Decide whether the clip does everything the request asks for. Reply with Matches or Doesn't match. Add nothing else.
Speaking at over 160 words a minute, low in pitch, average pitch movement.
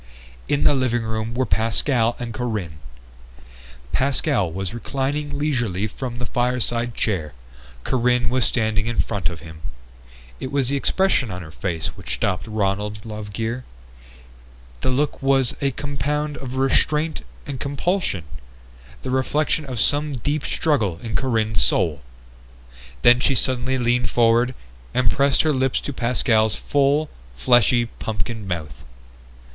Doesn't match